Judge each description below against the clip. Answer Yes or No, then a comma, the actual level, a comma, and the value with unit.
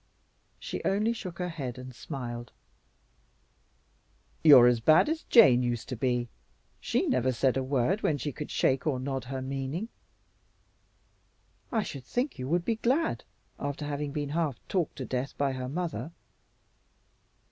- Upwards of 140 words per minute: Yes, average, 155 wpm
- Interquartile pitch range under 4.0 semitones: No, average, 4.9 semitones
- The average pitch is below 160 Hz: Yes, medium, 140 Hz